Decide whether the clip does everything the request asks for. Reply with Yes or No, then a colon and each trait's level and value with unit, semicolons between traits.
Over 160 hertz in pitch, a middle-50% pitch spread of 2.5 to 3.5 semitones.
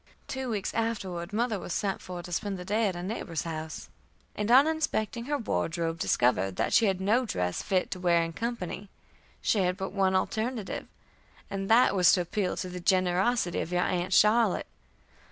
No: high, 190 Hz; average, 3.9 semitones